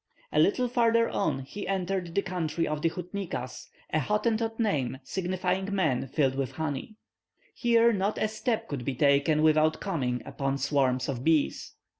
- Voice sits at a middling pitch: Yes, medium, 165 Hz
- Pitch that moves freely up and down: Yes, wide, 6.3 semitones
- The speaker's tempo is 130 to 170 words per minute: Yes, average, 160 wpm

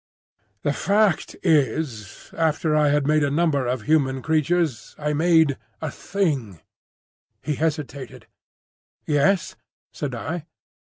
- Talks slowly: Yes, slow, 115 wpm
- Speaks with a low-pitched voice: No, medium, 150 Hz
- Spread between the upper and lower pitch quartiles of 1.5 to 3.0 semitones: Yes, average, 2.7 semitones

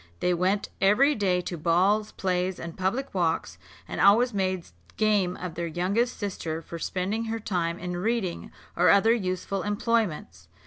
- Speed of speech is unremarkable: Yes, average, 160 wpm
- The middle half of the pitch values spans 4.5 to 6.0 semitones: No, average, 3.3 semitones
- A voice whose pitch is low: No, medium, 185 Hz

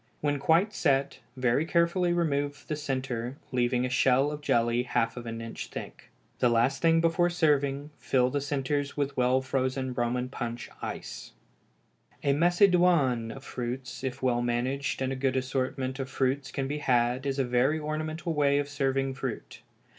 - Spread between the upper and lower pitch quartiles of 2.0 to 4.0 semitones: Yes, average, 2.7 semitones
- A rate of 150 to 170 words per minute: Yes, average, 165 wpm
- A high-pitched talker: No, low, 135 Hz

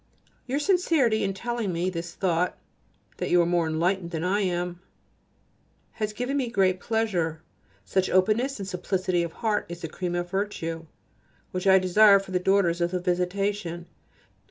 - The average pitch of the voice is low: No, medium, 185 Hz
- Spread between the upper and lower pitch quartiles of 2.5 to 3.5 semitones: Yes, average, 3.1 semitones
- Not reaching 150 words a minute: No, average, 165 wpm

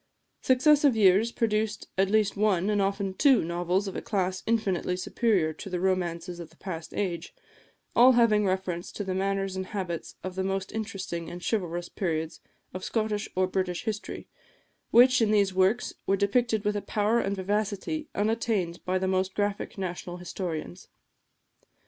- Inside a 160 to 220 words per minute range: Yes, average, 165 wpm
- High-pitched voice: Yes, high, 195 Hz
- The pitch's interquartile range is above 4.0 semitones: No, average, 2.7 semitones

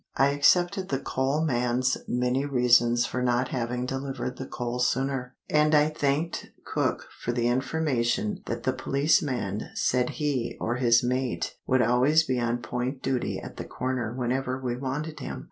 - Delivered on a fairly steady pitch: Yes, narrow, 2.3 semitones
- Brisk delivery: No, average, 160 wpm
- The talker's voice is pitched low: Yes, low, 130 Hz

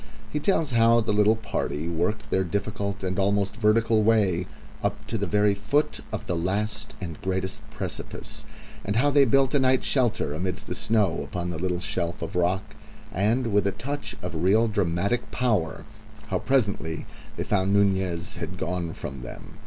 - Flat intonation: No, average, 4.0 semitones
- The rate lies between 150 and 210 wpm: Yes, average, 175 wpm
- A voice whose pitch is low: Yes, low, 100 Hz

